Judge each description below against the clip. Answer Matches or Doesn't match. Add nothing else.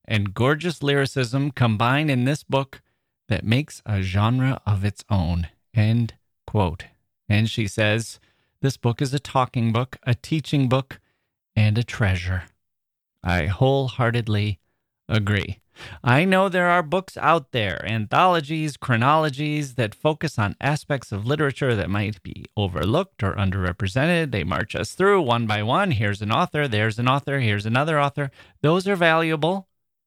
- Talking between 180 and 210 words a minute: Doesn't match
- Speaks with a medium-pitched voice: Doesn't match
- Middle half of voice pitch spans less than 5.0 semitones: Doesn't match